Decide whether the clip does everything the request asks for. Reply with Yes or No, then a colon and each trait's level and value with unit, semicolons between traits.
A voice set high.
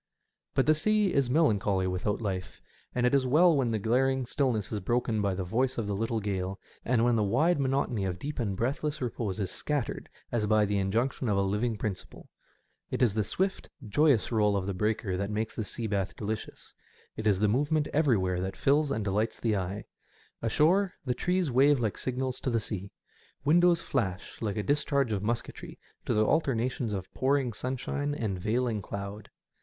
No: low, 115 Hz